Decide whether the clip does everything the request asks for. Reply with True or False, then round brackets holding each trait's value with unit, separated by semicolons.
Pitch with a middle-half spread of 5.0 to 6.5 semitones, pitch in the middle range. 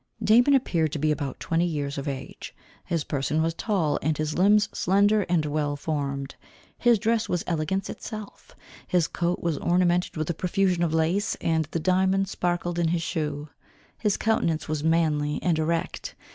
False (3.4 semitones; 165 Hz)